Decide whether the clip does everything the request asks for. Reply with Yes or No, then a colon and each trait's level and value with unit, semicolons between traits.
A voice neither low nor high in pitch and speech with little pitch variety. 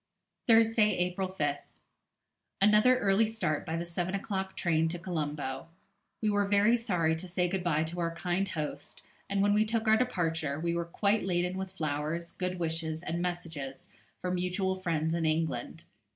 No: medium, 175 Hz; average, 3.3 semitones